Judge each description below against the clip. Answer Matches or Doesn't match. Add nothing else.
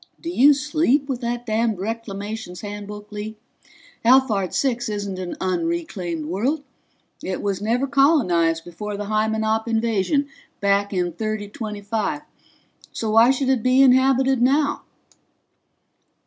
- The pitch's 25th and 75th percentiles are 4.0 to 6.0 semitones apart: Matches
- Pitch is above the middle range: Matches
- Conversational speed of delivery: Doesn't match